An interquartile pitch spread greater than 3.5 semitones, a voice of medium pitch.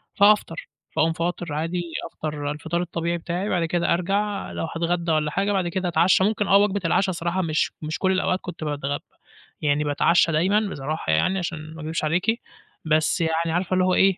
No: average, 3.0 semitones; medium, 170 Hz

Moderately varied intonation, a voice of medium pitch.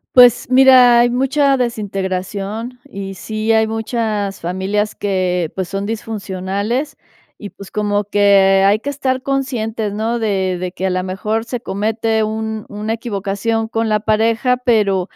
No: average, 3.0 semitones; high, 215 Hz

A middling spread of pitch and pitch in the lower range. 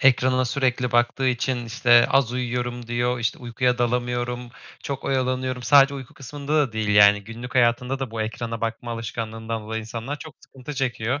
No: narrow, 2.0 semitones; low, 120 Hz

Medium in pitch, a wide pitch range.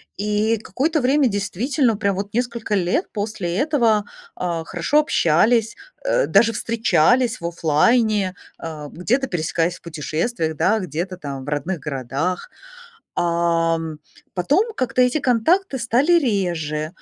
No: high, 205 Hz; wide, 6.7 semitones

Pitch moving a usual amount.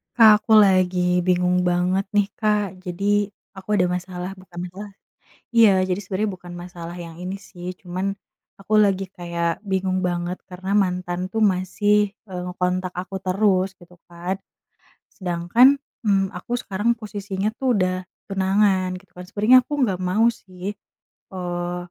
No: narrow, 2.2 semitones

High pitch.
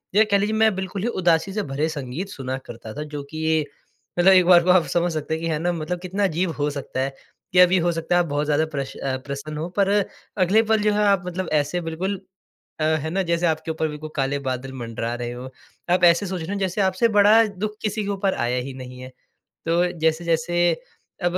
No: medium, 170 Hz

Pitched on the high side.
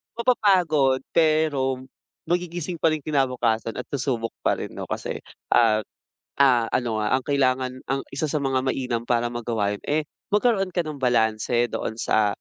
No: low, 130 Hz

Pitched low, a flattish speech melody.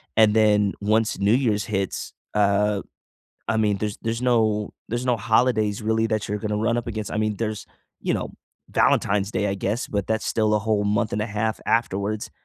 Yes: low, 105 Hz; narrow, 1.3 semitones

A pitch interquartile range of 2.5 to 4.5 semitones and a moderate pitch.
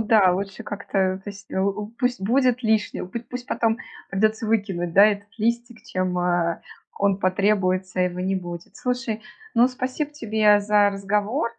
No: average, 3.5 semitones; high, 205 Hz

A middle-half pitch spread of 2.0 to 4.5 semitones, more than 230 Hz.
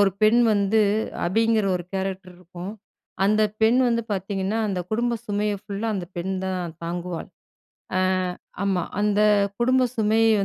No: average, 2.9 semitones; high, 200 Hz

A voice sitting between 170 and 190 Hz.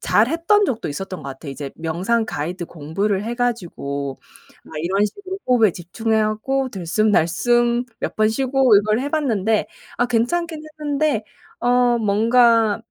No: high, 220 Hz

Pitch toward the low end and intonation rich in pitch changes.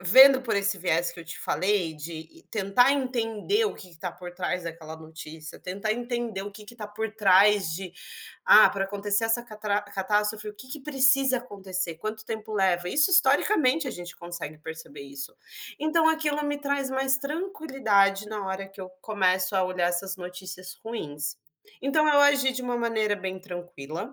No: high, 205 Hz; wide, 5.8 semitones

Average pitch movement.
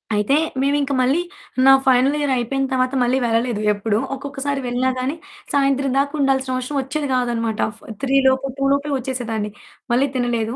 No: narrow, 2.2 semitones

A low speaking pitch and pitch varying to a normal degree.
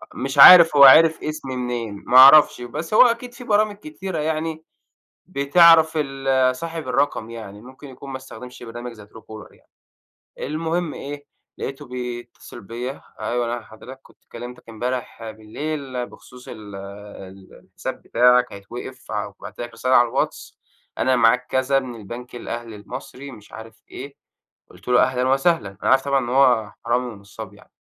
Yes: low, 125 Hz; average, 3.6 semitones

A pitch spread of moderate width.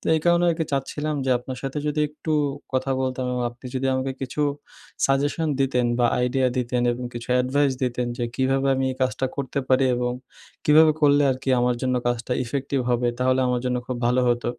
No: narrow, 2.0 semitones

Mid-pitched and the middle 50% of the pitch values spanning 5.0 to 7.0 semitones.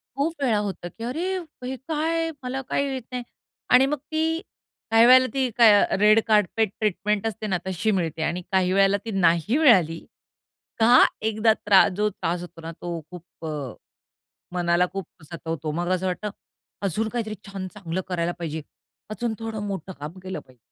No: high, 210 Hz; average, 5.3 semitones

